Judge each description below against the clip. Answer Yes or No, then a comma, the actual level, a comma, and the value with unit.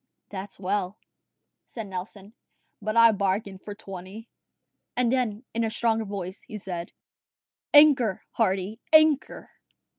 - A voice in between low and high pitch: No, high, 210 Hz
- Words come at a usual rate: No, slow, 120 wpm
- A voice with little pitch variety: No, average, 3.3 semitones